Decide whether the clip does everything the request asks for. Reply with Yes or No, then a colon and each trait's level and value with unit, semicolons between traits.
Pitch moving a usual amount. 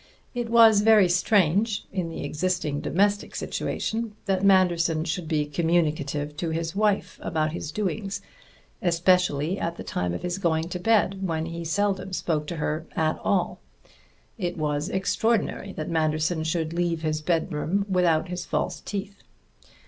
Yes: average, 3.7 semitones